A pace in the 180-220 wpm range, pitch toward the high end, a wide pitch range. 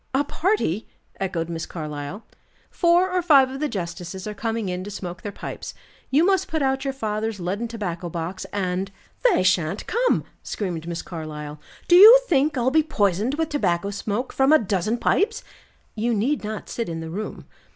Yes: average, 185 wpm; high, 210 Hz; wide, 7.6 semitones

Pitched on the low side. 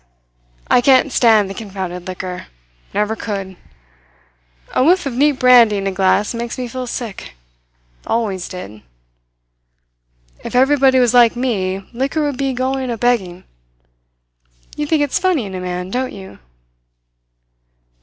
No: high, 235 Hz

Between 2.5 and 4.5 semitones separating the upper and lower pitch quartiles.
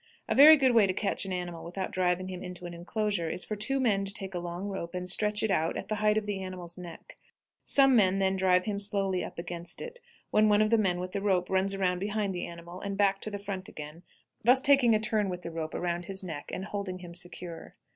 Yes: average, 2.8 semitones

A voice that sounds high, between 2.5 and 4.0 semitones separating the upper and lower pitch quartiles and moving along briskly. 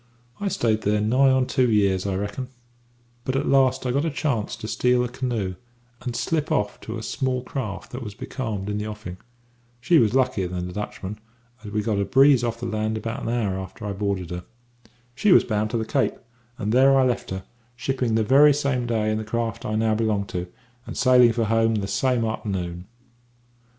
No: low, 115 Hz; average, 3.6 semitones; fast, 210 wpm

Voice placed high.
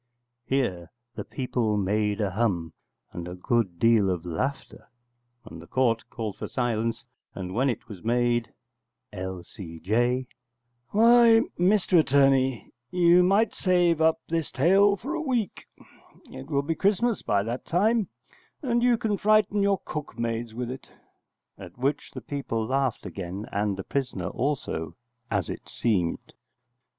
No: low, 125 Hz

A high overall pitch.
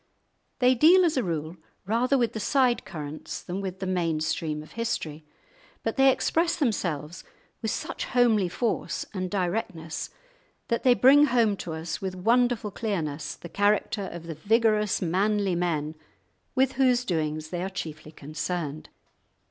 Yes: high, 195 Hz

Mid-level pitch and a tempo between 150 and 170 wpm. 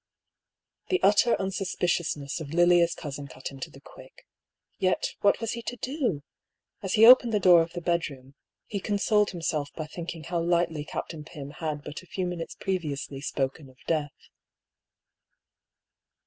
Yes: medium, 170 Hz; average, 160 wpm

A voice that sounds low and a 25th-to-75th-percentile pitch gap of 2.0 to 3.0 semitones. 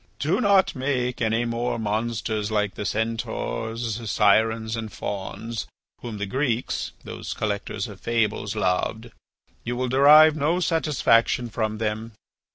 Yes: low, 115 Hz; narrow, 2.4 semitones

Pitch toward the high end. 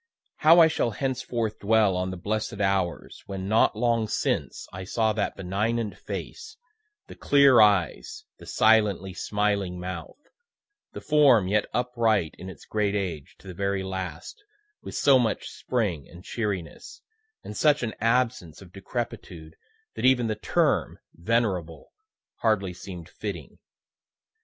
No: low, 105 Hz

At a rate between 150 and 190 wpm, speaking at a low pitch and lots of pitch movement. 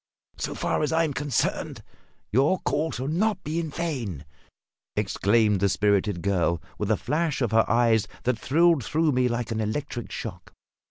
Yes: average, 170 wpm; low, 125 Hz; wide, 6.4 semitones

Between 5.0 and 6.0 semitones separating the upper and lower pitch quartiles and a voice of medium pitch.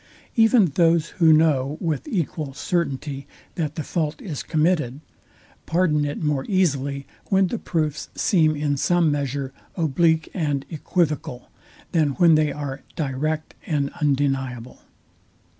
No: average, 3.0 semitones; medium, 150 Hz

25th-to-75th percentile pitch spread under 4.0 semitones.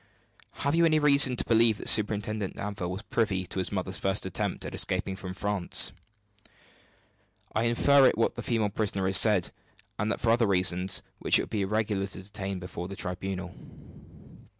Yes: average, 2.9 semitones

